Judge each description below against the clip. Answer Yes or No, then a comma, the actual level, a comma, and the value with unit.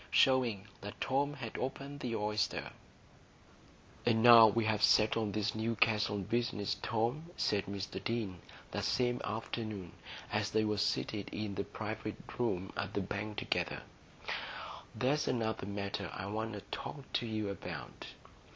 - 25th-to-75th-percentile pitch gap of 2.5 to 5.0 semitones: Yes, average, 2.8 semitones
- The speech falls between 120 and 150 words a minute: Yes, average, 140 wpm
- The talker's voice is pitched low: Yes, low, 110 Hz